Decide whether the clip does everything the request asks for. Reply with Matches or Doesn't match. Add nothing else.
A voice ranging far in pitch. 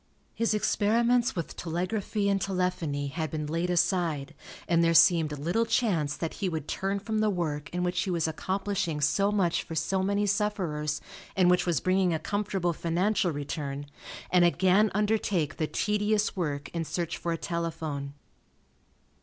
Doesn't match